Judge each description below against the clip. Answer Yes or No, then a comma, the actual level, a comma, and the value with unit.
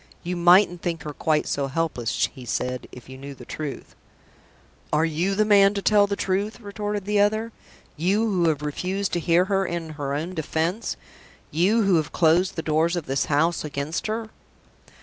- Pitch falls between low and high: Yes, medium, 170 Hz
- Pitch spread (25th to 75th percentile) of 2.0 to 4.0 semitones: No, average, 4.7 semitones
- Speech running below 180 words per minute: No, average, 190 wpm